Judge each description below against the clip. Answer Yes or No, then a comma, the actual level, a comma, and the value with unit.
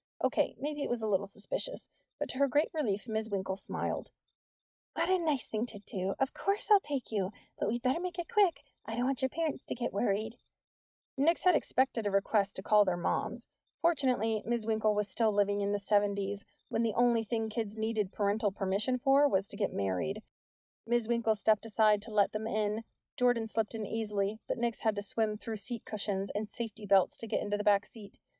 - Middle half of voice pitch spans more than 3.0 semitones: Yes, average, 3.4 semitones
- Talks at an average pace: No, fast, 210 wpm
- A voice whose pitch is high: Yes, high, 220 Hz